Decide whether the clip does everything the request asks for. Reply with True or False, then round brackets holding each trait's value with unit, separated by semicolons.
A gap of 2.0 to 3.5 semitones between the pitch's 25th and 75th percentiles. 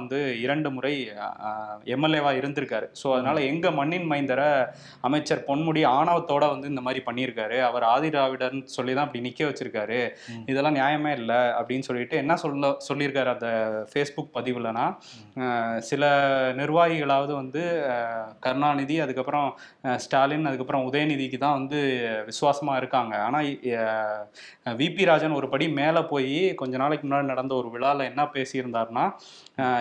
True (2.8 semitones)